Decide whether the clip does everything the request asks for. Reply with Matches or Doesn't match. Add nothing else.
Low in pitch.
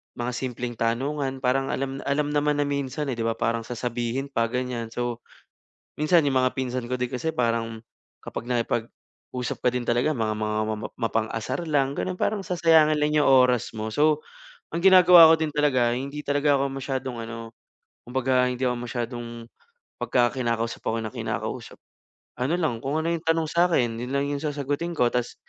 Matches